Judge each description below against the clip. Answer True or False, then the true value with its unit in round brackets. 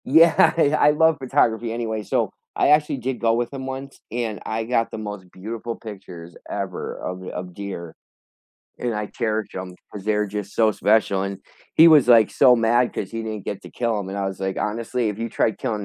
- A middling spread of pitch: True (3.3 semitones)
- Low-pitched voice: True (110 Hz)